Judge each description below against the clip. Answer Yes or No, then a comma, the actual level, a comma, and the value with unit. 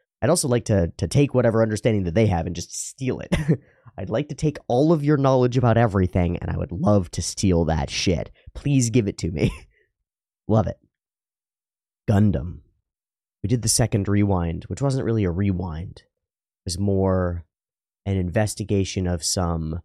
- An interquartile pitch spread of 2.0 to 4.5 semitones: No, average, 4.9 semitones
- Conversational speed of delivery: Yes, average, 175 wpm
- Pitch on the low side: Yes, low, 100 Hz